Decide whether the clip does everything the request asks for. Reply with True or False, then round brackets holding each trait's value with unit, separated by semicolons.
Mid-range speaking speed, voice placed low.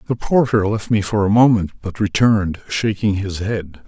True (185 wpm; 105 Hz)